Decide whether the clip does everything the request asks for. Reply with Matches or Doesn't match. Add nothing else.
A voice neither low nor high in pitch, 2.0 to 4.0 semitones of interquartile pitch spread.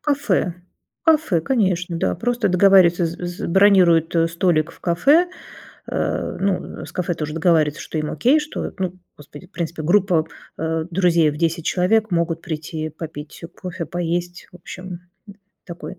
Matches